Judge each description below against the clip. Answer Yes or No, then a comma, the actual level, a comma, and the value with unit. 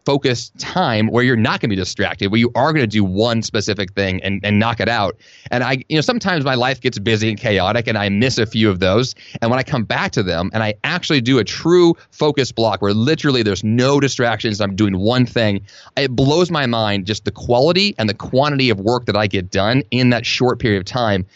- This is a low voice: Yes, low, 115 Hz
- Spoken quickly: Yes, fast, 240 wpm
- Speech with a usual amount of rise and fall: Yes, average, 4.1 semitones